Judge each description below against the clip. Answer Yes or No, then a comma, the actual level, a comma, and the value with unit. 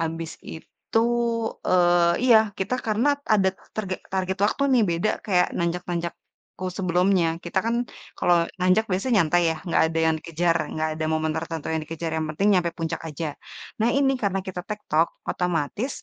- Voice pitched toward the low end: No, medium, 175 Hz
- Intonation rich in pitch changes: No, average, 3.3 semitones